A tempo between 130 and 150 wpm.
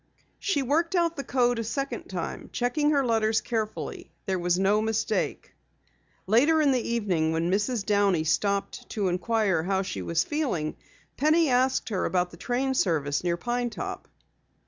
No: average, 165 wpm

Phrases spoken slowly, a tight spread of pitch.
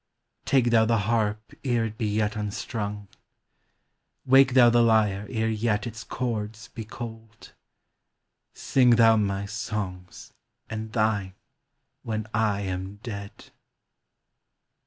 Yes: slow, 125 wpm; narrow, 2.1 semitones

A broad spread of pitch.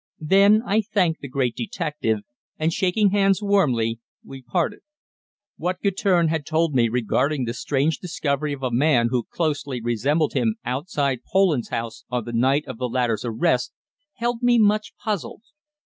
Yes: wide, 7.0 semitones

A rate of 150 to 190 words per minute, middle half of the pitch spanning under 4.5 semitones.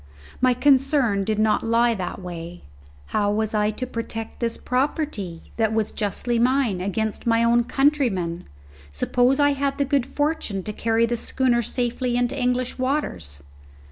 Yes: average, 155 wpm; average, 3.6 semitones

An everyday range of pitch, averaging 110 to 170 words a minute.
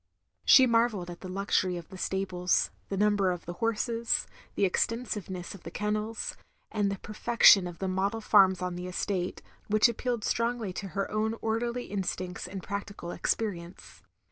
Yes: average, 3.4 semitones; average, 165 wpm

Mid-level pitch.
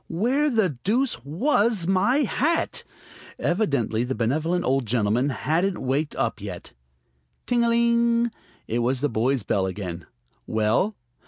Yes: medium, 160 Hz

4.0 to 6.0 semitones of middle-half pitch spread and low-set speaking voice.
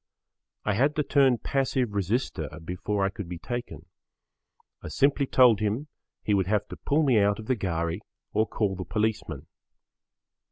Yes: average, 4.9 semitones; low, 105 Hz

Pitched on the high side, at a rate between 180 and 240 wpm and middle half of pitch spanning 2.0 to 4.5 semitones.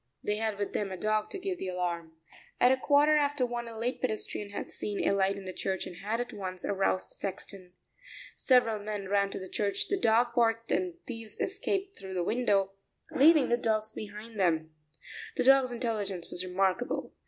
Yes: high, 215 Hz; average, 200 wpm; average, 4.2 semitones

